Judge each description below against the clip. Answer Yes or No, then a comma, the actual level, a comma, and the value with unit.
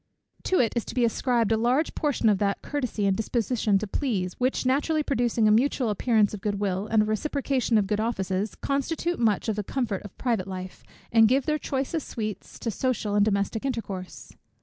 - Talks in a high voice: Yes, high, 225 Hz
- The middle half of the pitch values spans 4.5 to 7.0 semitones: No, average, 4.0 semitones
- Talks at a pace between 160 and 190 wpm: No, average, 200 wpm